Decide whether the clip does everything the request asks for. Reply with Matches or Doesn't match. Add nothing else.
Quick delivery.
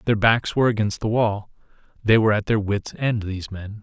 Matches